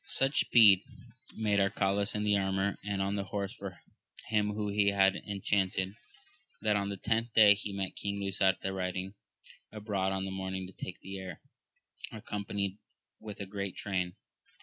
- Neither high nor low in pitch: No, low, 100 Hz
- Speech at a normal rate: Yes, average, 170 wpm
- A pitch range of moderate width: No, narrow, 1.3 semitones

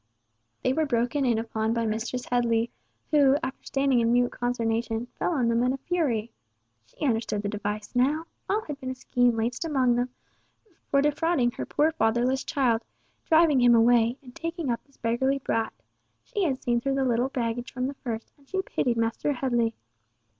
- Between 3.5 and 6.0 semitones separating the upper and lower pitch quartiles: No, average, 3.1 semitones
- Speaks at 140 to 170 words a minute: No, average, 185 wpm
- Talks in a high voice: Yes, high, 245 Hz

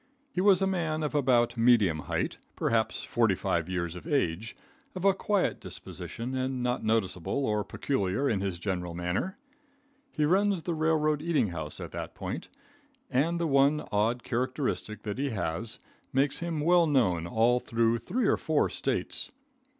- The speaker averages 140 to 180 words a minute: Yes, average, 160 wpm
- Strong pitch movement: Yes, wide, 7.0 semitones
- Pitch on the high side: No, low, 125 Hz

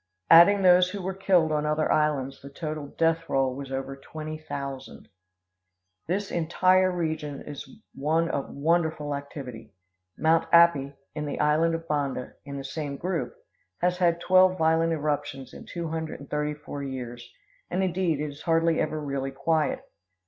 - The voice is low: No, medium, 155 Hz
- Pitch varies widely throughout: No, average, 3.1 semitones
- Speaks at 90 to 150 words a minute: No, average, 165 wpm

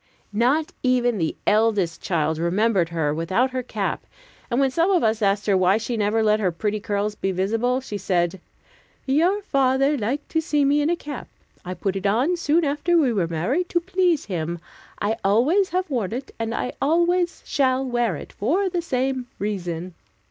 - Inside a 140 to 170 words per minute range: No, average, 190 wpm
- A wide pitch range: Yes, wide, 6.8 semitones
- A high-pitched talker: Yes, high, 235 Hz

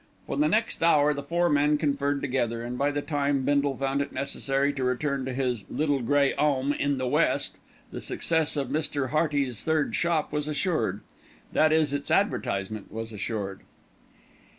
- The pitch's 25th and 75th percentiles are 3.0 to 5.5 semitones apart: No, narrow, 2.4 semitones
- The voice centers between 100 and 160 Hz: Yes, medium, 140 Hz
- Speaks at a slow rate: No, average, 175 wpm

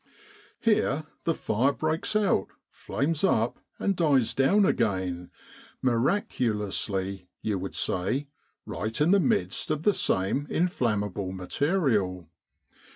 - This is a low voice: Yes, low, 125 Hz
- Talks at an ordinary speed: No, slow, 110 wpm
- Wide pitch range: Yes, wide, 8.7 semitones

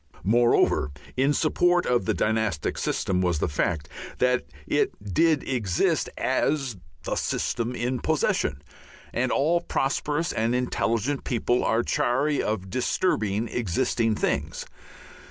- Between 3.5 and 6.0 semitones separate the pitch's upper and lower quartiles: Yes, average, 4.3 semitones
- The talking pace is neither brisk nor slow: No, slow, 120 wpm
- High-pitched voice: No, low, 120 Hz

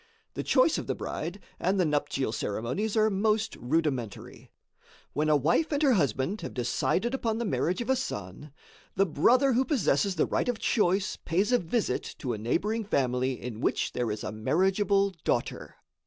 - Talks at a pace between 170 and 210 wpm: Yes, average, 180 wpm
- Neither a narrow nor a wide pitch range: No, wide, 8.8 semitones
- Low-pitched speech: No, medium, 180 Hz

